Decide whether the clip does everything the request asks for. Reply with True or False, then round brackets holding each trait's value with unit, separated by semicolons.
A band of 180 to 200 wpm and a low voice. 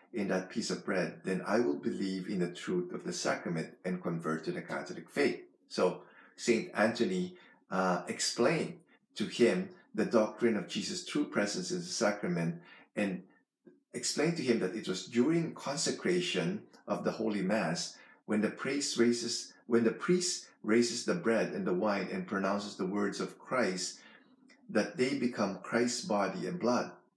False (170 wpm; 105 Hz)